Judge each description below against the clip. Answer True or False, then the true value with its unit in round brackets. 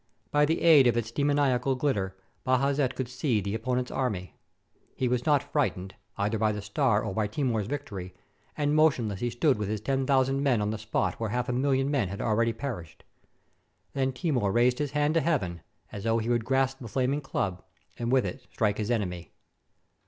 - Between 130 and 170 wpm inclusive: False (195 wpm)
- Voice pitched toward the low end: True (125 Hz)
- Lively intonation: False (4.3 semitones)